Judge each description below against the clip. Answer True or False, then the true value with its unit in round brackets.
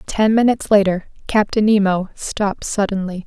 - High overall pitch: True (205 Hz)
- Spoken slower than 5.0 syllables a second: False (5.2 syllables/s)